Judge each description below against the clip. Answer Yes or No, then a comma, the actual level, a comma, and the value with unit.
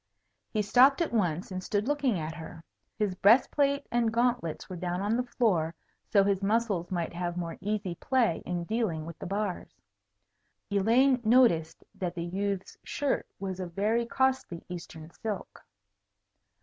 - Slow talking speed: No, average, 160 wpm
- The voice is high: Yes, high, 200 Hz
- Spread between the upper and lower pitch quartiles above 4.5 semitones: Yes, average, 5.2 semitones